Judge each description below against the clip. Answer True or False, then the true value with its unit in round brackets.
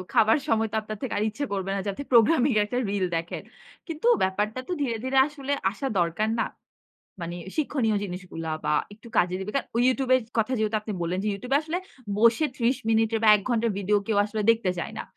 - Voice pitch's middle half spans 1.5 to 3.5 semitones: False (4.2 semitones)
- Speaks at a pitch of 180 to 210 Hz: False (220 Hz)